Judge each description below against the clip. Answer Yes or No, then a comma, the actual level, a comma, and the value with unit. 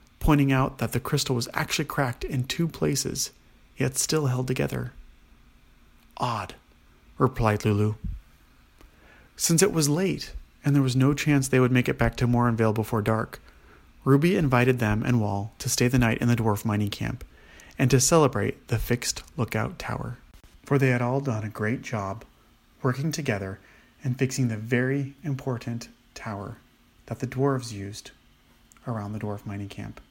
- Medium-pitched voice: No, low, 120 Hz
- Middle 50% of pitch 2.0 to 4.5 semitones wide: Yes, average, 4.0 semitones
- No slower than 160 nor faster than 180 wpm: Yes, average, 165 wpm